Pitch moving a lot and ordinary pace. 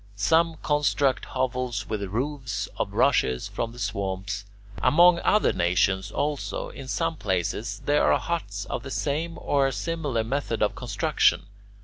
Yes: wide, 6.6 semitones; average, 145 wpm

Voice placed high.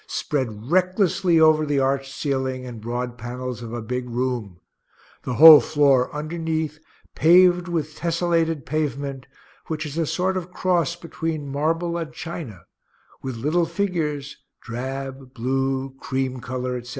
No: medium, 145 Hz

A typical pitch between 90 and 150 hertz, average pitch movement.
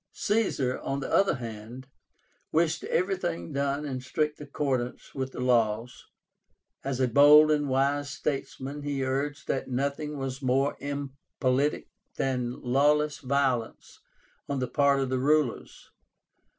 No: medium, 140 Hz; narrow, 2.2 semitones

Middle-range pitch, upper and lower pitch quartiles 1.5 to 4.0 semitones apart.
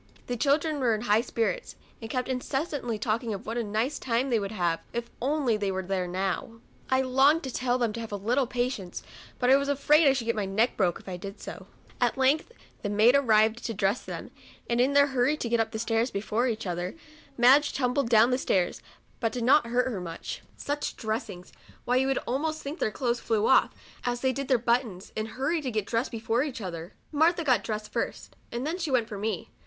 No: high, 235 Hz; average, 3.6 semitones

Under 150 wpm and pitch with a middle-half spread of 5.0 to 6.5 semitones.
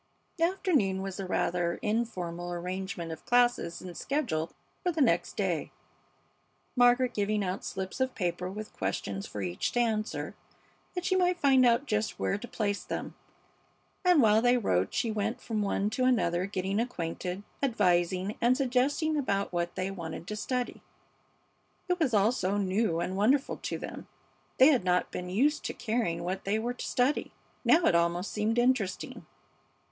No: average, 170 wpm; wide, 5.5 semitones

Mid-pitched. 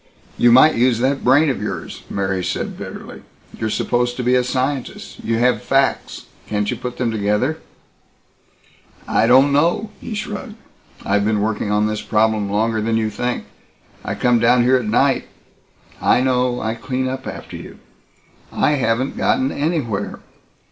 No: low, 125 Hz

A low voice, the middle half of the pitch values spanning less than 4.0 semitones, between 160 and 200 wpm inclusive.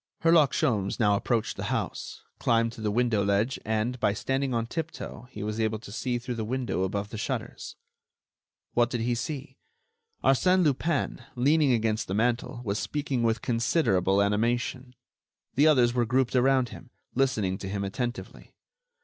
Yes: low, 120 Hz; average, 3.4 semitones; average, 165 wpm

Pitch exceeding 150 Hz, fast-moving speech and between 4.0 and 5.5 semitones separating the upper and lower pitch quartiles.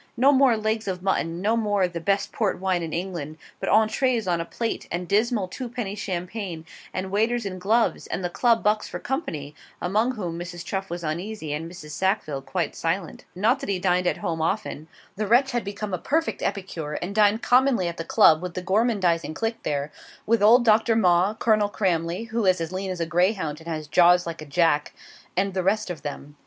Yes: high, 190 Hz; fast, 210 wpm; average, 4.3 semitones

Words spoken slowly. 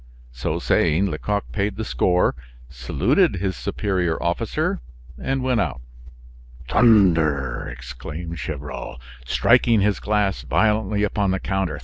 Yes: slow, 115 wpm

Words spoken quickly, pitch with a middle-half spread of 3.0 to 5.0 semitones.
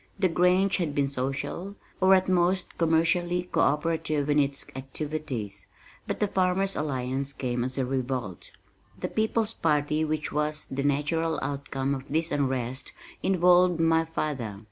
No: average, 145 wpm; average, 4.5 semitones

